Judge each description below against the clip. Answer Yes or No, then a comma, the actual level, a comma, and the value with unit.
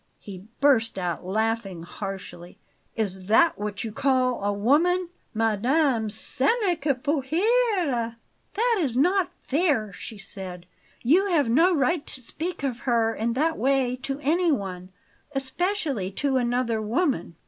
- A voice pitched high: Yes, very high, 255 Hz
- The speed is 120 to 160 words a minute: Yes, average, 140 wpm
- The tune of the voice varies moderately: No, wide, 6.8 semitones